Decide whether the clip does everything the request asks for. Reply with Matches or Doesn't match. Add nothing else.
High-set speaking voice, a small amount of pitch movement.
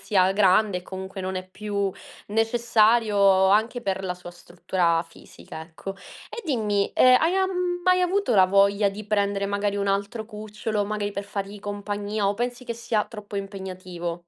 Matches